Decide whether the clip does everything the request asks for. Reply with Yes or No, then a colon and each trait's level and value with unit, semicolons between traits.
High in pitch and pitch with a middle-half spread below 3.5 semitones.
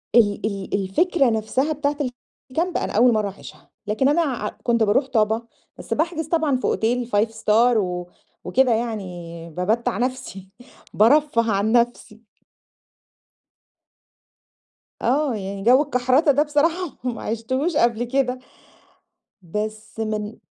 No: high, 235 Hz; average, 4.2 semitones